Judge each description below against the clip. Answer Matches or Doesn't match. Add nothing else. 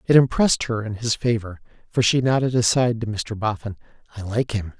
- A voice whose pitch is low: Matches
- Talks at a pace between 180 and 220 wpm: Matches